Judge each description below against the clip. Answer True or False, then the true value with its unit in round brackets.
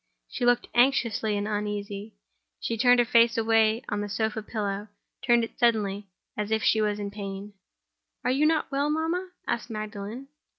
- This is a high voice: True (220 Hz)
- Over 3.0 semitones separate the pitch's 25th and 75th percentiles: False (2.7 semitones)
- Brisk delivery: False (165 wpm)